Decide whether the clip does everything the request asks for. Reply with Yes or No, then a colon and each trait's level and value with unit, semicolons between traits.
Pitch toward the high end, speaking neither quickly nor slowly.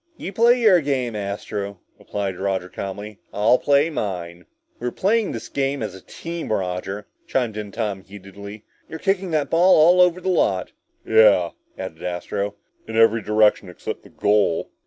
No: low, 105 Hz; average, 160 wpm